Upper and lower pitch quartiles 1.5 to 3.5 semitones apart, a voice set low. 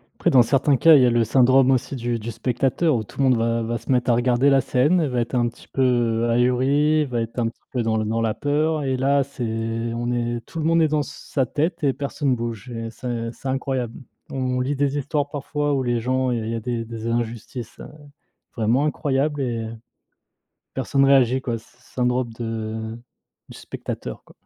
Yes: average, 3.0 semitones; low, 125 Hz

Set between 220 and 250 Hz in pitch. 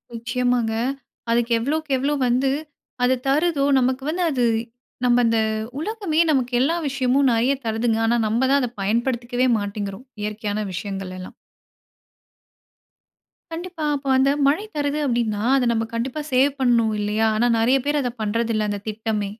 Yes: high, 245 Hz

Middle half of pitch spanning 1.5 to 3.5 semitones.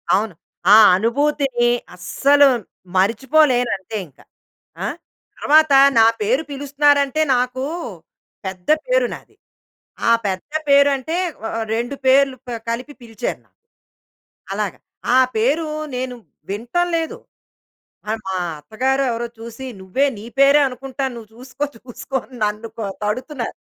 No: average, 4.1 semitones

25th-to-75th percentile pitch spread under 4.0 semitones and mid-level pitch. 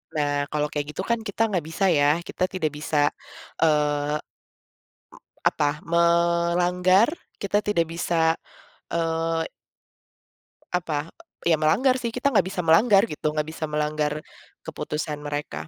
Yes: average, 3.2 semitones; medium, 165 Hz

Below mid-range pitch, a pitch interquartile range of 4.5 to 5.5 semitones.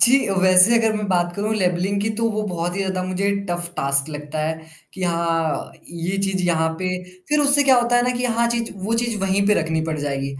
No: medium, 185 Hz; average, 5.2 semitones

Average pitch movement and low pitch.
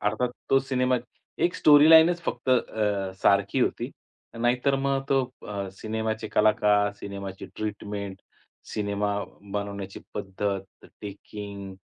Yes: average, 3.8 semitones; low, 105 Hz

